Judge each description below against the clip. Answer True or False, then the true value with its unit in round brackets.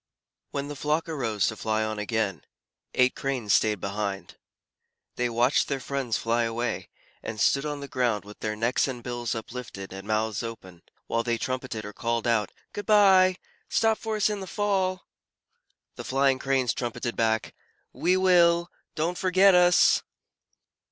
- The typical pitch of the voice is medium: False (125 Hz)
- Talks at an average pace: True (160 wpm)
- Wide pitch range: True (7.1 semitones)